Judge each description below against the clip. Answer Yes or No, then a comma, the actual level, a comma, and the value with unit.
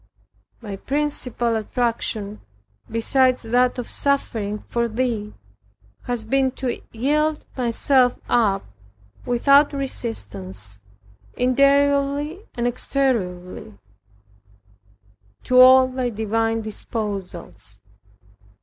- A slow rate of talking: Yes, slow, 80 wpm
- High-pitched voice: Yes, high, 240 Hz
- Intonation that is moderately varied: Yes, average, 3.7 semitones